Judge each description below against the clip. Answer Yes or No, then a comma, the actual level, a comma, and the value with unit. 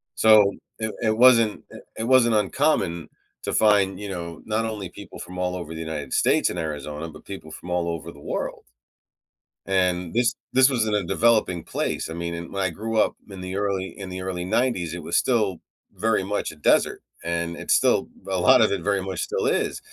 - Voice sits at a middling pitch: No, very low, 95 Hz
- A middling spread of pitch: Yes, average, 4.1 semitones